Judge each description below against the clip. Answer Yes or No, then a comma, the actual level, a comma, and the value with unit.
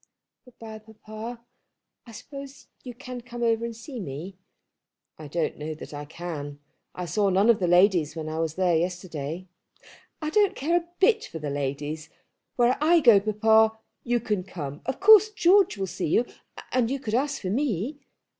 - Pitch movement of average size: No, wide, 6.9 semitones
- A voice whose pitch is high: Yes, high, 215 Hz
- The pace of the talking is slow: No, average, 185 wpm